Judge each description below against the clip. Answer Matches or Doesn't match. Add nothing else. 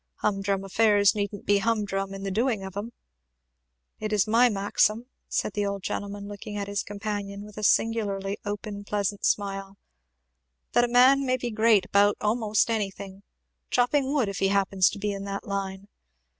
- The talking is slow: Doesn't match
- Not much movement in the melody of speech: Matches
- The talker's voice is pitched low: Doesn't match